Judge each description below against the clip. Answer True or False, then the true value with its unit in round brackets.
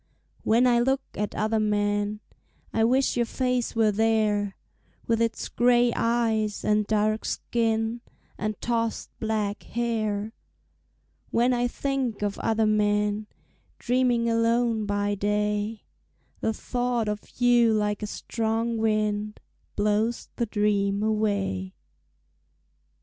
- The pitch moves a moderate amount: False (2.0 semitones)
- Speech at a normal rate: False (115 wpm)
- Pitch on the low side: False (220 Hz)